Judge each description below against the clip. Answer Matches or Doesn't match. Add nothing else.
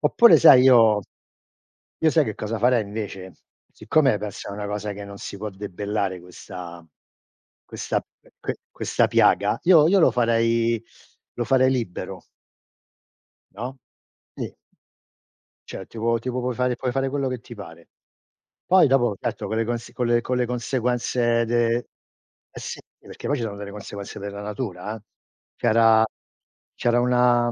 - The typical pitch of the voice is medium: Doesn't match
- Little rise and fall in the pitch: Doesn't match